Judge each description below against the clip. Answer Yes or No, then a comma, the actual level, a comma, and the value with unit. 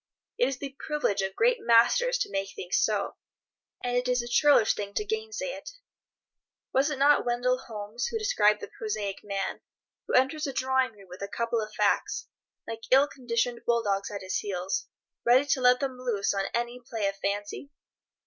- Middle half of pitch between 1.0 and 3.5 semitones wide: No, average, 4.9 semitones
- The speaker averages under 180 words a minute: No, average, 190 wpm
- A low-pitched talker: No, high, 240 Hz